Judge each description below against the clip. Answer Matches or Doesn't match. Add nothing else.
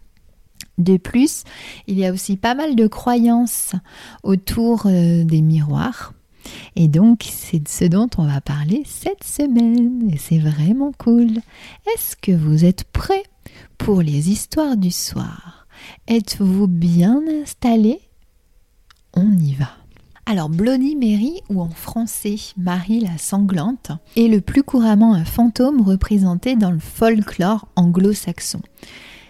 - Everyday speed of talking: Doesn't match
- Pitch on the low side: Doesn't match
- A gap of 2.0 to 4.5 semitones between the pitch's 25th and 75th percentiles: Doesn't match